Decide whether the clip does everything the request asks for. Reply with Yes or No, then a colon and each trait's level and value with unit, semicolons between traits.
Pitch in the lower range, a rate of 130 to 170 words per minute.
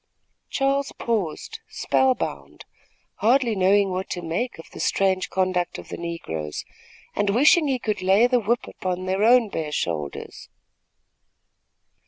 No: high, 195 Hz; average, 140 wpm